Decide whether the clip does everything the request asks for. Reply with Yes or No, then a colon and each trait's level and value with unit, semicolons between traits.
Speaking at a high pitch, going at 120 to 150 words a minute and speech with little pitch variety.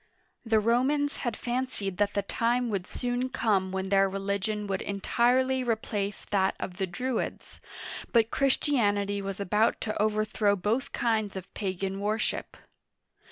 No: high, 210 Hz; average, 140 wpm; average, 3.4 semitones